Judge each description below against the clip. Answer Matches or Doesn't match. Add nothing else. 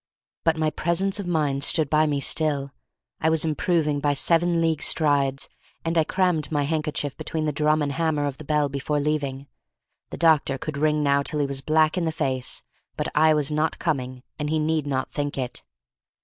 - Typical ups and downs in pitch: Doesn't match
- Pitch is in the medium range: Matches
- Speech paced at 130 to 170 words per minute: Doesn't match